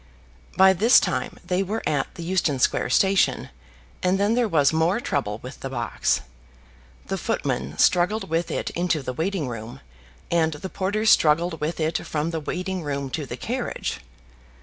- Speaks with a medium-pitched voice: Yes, medium, 165 Hz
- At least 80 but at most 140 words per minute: No, average, 170 wpm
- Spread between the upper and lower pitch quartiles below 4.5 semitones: No, average, 4.8 semitones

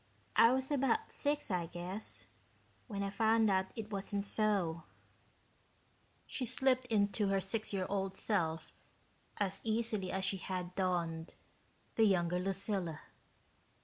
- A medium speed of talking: No, slow, 130 wpm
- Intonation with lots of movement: No, average, 3.3 semitones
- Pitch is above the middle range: Yes, high, 195 Hz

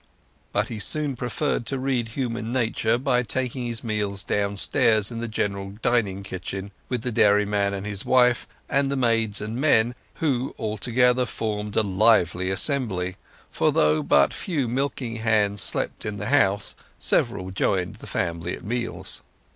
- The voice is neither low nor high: No, low, 110 Hz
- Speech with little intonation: No, average, 3.7 semitones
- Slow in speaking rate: No, average, 160 wpm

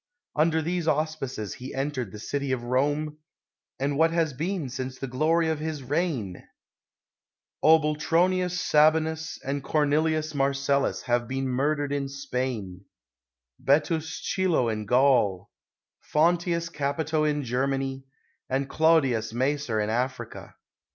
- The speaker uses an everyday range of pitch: Yes, average, 3.4 semitones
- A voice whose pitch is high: No, medium, 140 Hz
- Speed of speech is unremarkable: No, slow, 130 wpm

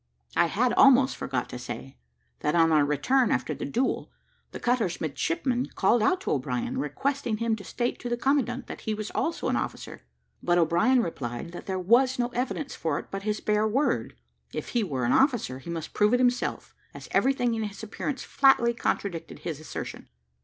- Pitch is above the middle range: Yes, high, 220 Hz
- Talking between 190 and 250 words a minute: Yes, average, 195 wpm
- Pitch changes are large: Yes, wide, 6.9 semitones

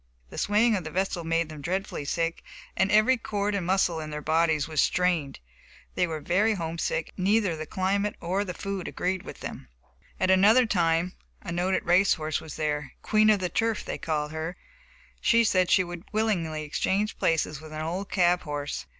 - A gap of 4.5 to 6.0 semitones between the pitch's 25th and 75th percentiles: No, average, 3.9 semitones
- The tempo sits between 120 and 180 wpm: No, average, 195 wpm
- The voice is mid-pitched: Yes, medium, 180 Hz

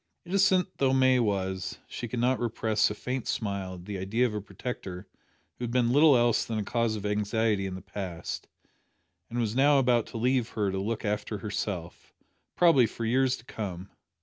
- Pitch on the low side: Yes, low, 110 Hz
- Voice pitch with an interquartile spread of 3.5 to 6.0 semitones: Yes, average, 3.8 semitones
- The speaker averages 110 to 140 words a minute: No, average, 195 wpm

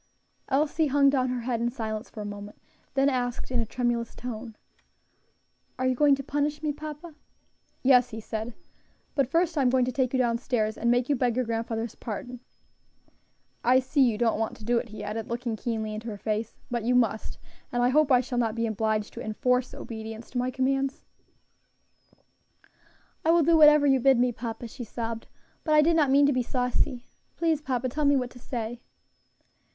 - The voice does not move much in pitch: No, average, 3.1 semitones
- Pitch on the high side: Yes, high, 245 Hz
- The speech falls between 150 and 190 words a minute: No, average, 200 wpm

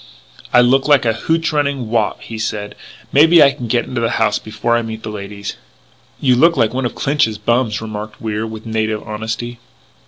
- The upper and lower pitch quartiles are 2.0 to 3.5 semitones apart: Yes, average, 3.1 semitones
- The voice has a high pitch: No, low, 115 Hz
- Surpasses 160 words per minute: Yes, average, 200 wpm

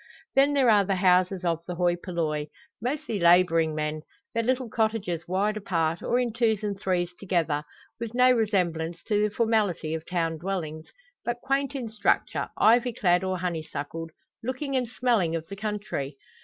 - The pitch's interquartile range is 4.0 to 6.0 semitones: Yes, average, 5.2 semitones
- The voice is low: No, high, 190 Hz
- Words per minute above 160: Yes, average, 170 wpm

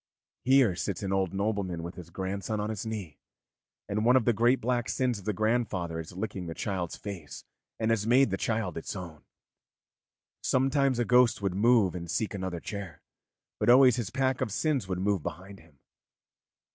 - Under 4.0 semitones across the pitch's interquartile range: No, average, 4.5 semitones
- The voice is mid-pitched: No, low, 100 Hz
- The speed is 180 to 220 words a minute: Yes, average, 185 wpm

